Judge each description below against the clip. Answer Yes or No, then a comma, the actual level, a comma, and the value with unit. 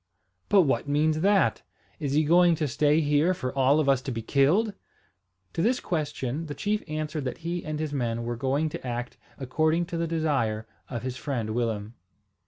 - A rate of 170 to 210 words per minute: Yes, average, 190 wpm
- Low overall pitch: No, medium, 150 Hz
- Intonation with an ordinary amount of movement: Yes, average, 4.2 semitones